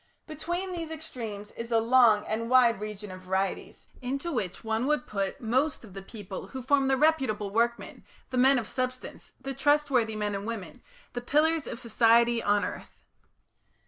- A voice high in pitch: Yes, high, 235 Hz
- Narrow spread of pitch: No, average, 4.3 semitones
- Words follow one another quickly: No, average, 175 wpm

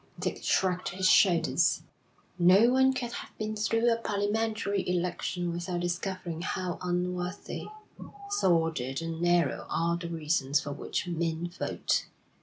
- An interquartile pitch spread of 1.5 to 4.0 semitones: Yes, average, 2.9 semitones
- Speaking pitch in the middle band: Yes, medium, 180 Hz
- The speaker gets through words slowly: Yes, slow, 130 wpm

